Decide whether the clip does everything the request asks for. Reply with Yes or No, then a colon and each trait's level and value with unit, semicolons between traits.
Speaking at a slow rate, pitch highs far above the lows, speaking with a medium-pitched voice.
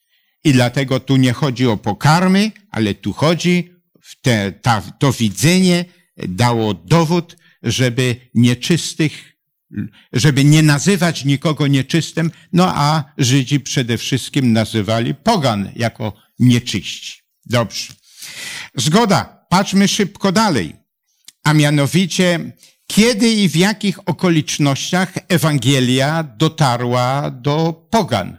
Yes: slow, 105 wpm; wide, 5.9 semitones; medium, 150 Hz